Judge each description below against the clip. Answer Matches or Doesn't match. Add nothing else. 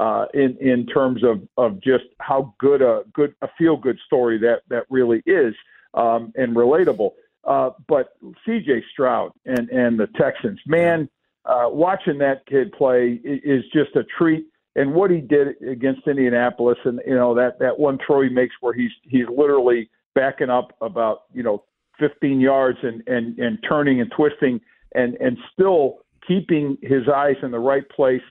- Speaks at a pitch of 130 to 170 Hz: Matches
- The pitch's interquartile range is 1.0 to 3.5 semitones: Doesn't match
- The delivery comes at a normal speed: Matches